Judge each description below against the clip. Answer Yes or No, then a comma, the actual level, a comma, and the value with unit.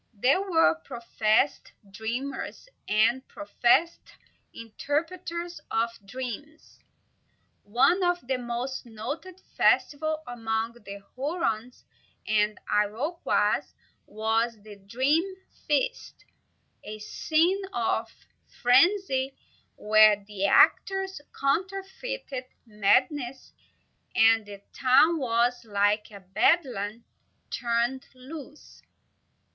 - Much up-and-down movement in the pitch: Yes, wide, 6.3 semitones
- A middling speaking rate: No, slow, 85 wpm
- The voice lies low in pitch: No, high, 245 Hz